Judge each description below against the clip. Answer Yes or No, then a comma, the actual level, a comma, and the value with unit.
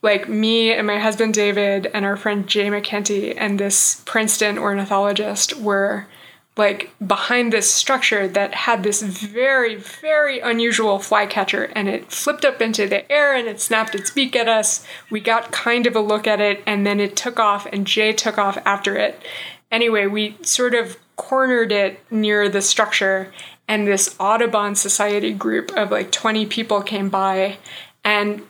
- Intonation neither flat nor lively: No, narrow, 2.1 semitones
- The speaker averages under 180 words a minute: Yes, average, 170 wpm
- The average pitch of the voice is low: No, high, 210 Hz